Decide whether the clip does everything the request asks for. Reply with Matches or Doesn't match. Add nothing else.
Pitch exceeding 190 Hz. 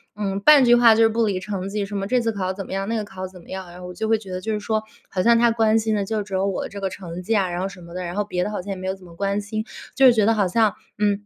Matches